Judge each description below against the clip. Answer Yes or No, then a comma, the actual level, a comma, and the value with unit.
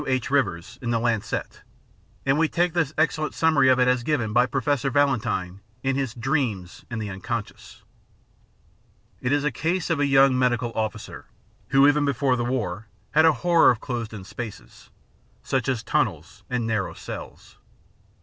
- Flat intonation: No, average, 4.0 semitones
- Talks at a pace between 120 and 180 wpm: Yes, average, 170 wpm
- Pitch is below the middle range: Yes, low, 130 Hz